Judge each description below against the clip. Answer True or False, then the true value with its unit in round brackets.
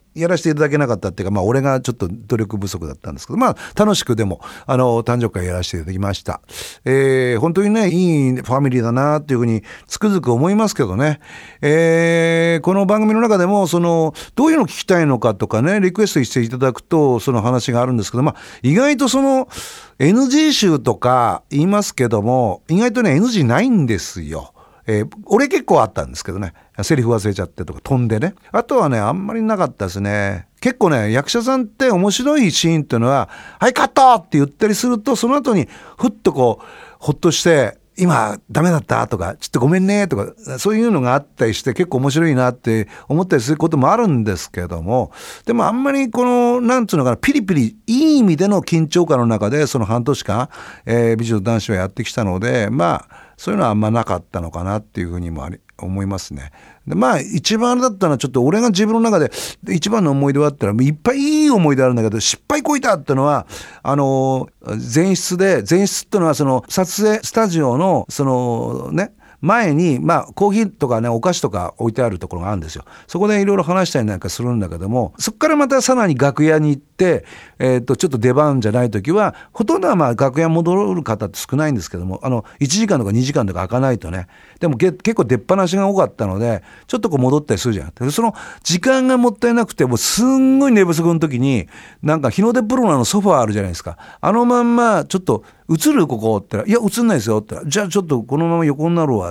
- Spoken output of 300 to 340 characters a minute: False (455 characters per minute)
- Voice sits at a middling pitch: True (145 Hz)